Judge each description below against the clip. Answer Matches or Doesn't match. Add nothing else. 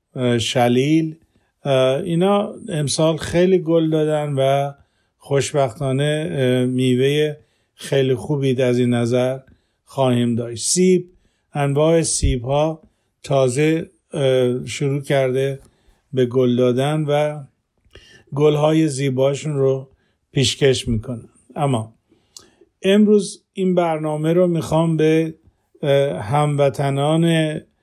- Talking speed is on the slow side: Matches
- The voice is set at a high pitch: Doesn't match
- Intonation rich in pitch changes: Doesn't match